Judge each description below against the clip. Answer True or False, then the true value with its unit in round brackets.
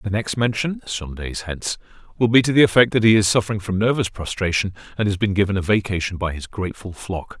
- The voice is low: True (100 Hz)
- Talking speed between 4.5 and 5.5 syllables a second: False (6.2 syllables/s)